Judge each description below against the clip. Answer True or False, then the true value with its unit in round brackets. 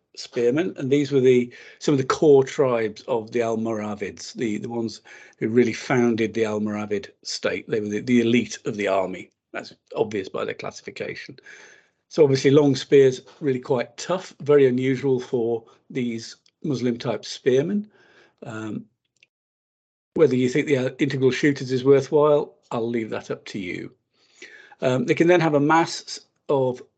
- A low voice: True (130 Hz)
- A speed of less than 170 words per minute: True (160 wpm)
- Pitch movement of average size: True (3.4 semitones)